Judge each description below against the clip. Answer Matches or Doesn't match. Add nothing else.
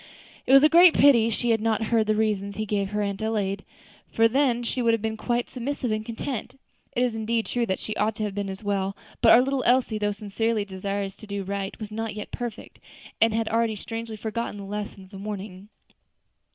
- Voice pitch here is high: Matches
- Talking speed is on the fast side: Matches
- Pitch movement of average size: Doesn't match